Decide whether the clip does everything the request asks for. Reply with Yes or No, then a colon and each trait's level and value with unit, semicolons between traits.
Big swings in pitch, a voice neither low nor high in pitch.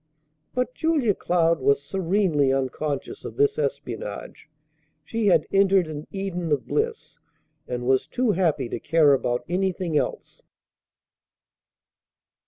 Yes: wide, 5.8 semitones; medium, 175 Hz